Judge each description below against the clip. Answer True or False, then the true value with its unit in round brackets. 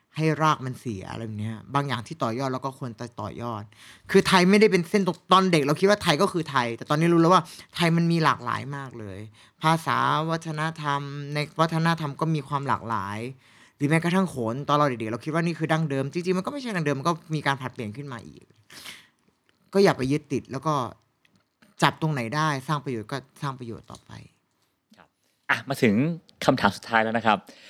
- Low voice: False (145 Hz)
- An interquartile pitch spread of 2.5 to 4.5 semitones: False (5.3 semitones)